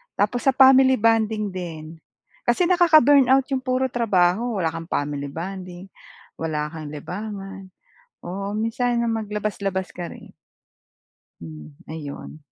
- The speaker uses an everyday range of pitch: No, wide, 6.0 semitones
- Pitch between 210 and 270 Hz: No, high, 200 Hz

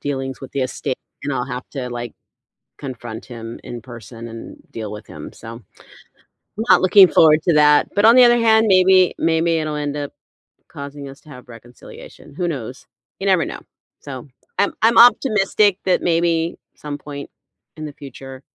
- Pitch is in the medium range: Yes, medium, 145 Hz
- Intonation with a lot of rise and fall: Yes, wide, 5.7 semitones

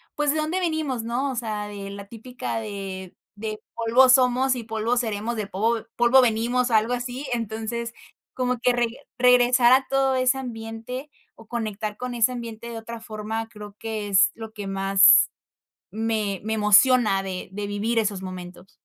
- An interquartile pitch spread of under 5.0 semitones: Yes, average, 3.0 semitones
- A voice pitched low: No, high, 225 Hz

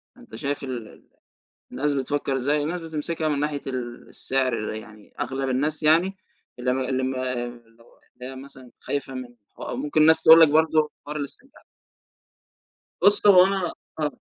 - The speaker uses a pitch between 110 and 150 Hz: Yes, medium, 140 Hz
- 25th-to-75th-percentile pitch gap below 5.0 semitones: Yes, average, 3.4 semitones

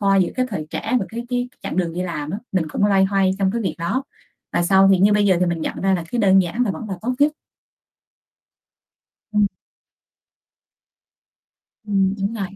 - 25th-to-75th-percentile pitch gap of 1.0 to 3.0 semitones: Yes, average, 2.7 semitones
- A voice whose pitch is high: Yes, high, 195 Hz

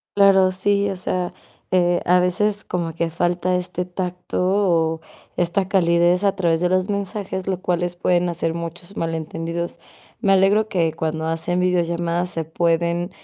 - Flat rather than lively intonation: Yes, narrow, 1.8 semitones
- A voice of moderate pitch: Yes, medium, 175 Hz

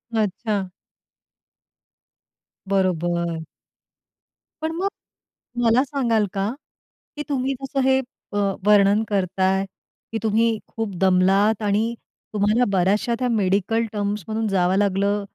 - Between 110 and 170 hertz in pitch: No, high, 205 Hz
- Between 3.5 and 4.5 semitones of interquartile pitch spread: No, average, 3.0 semitones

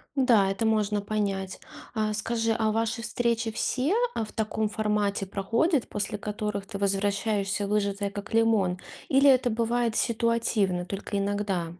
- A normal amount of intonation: No, narrow, 2.2 semitones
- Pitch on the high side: Yes, high, 210 Hz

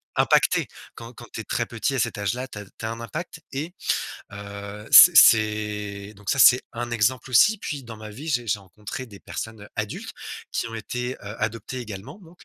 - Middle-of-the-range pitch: No, low, 115 Hz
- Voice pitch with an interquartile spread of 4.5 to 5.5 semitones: No, average, 3.6 semitones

